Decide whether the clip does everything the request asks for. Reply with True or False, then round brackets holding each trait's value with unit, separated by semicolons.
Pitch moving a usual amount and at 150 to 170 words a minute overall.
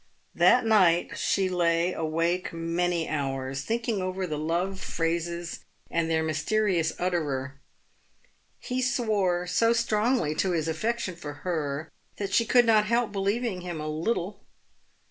False (4.6 semitones; 135 wpm)